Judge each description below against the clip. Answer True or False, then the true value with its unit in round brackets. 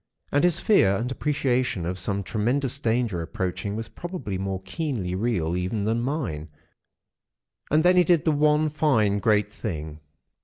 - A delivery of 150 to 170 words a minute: True (155 wpm)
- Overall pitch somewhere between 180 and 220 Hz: False (115 Hz)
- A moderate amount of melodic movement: False (7.5 semitones)